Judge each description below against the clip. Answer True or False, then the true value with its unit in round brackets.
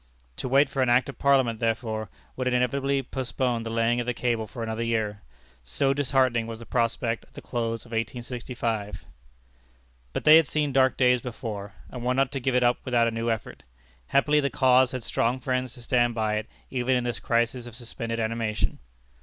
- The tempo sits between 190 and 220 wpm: True (200 wpm)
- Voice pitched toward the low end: True (120 Hz)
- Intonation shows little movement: True (2.1 semitones)